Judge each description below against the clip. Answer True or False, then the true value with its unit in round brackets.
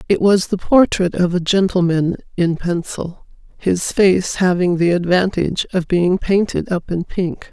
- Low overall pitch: False (180 Hz)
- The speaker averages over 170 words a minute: False (160 wpm)